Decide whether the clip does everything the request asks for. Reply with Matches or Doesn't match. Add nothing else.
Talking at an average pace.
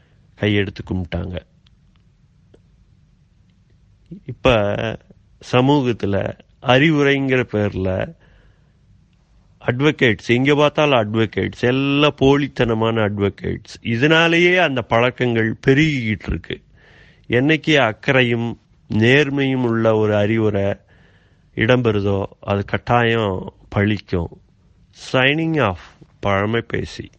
Doesn't match